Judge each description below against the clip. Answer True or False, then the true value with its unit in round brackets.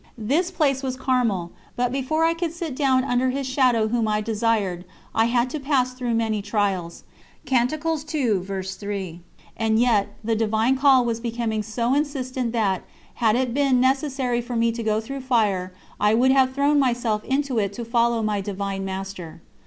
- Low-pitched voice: False (235 Hz)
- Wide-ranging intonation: False (3.7 semitones)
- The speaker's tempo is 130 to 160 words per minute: False (170 wpm)